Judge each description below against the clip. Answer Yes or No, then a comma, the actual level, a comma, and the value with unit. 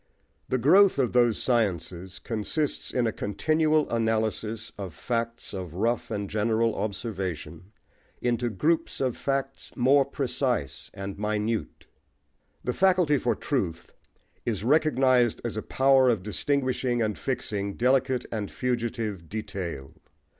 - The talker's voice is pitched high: No, low, 115 Hz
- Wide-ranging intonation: No, average, 4.1 semitones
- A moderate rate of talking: No, slow, 125 wpm